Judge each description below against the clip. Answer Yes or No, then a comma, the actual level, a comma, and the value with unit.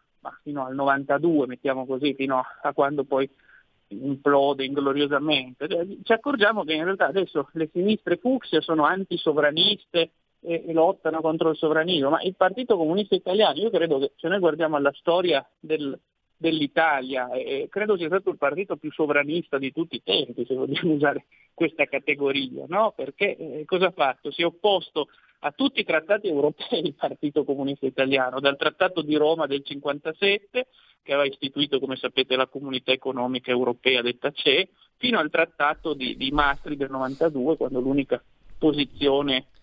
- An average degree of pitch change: Yes, average, 3.7 semitones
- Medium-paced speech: Yes, average, 160 wpm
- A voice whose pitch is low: No, medium, 150 Hz